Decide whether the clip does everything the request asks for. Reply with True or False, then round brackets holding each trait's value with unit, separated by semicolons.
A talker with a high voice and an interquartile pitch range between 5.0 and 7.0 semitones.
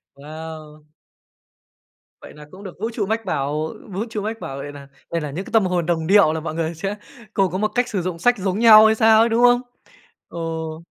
False (180 Hz; 5.5 semitones)